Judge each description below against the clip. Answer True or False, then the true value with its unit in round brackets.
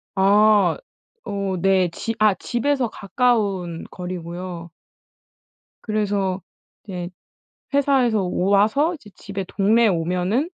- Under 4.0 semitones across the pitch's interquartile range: True (3.4 semitones)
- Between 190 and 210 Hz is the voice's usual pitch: True (200 Hz)